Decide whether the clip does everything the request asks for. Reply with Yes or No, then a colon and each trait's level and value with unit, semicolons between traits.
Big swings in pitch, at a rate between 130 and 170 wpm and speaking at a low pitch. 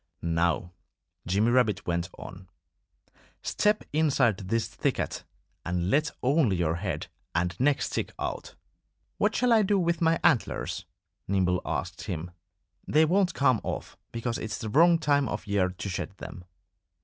Yes: wide, 9.0 semitones; average, 150 wpm; low, 110 Hz